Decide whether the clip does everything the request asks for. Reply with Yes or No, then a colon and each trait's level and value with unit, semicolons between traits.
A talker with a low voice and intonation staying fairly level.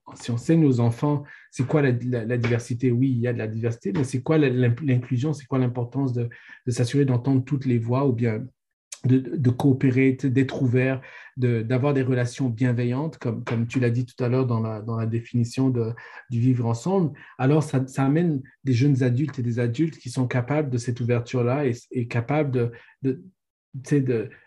Yes: low, 130 Hz; narrow, 2.1 semitones